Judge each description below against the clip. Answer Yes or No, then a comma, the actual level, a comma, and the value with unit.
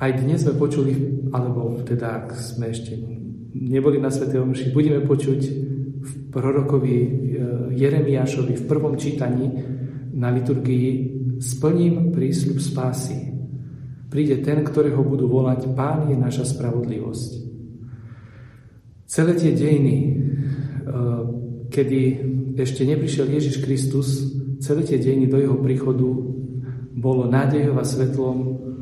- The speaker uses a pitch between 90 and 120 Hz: No, low, 130 Hz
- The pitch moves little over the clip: Yes, narrow, 1.5 semitones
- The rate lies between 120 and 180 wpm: No, slow, 110 wpm